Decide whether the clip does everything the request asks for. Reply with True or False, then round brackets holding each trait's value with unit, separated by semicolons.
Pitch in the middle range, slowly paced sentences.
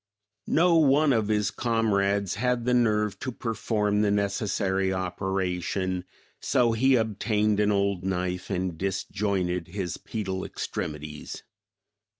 False (100 Hz; 120 wpm)